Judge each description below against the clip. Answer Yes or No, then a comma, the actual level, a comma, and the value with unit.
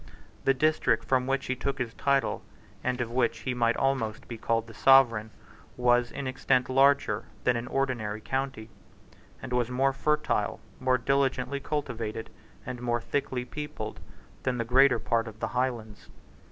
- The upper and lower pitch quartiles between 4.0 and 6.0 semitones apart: No, narrow, 2.5 semitones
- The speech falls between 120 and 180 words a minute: Yes, average, 160 wpm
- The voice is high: No, low, 125 Hz